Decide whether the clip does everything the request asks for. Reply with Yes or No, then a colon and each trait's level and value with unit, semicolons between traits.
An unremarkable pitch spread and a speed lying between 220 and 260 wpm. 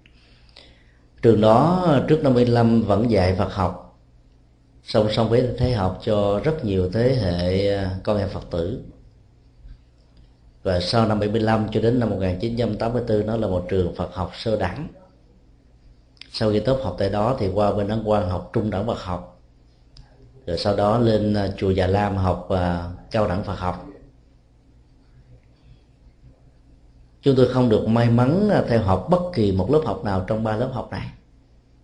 No: average, 4.6 semitones; slow, 165 wpm